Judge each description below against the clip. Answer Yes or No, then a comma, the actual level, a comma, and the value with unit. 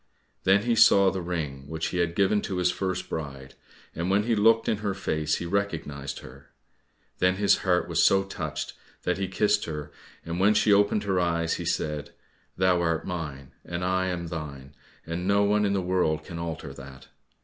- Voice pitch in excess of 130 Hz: No, very low, 90 Hz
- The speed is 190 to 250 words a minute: Yes, average, 195 wpm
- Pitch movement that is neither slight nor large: Yes, average, 3.8 semitones